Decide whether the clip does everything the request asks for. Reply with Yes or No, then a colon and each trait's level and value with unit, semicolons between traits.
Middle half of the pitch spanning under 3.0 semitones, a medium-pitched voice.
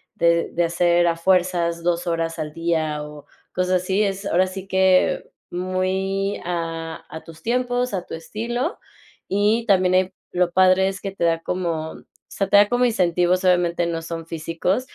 Yes: narrow, 2.4 semitones; medium, 180 Hz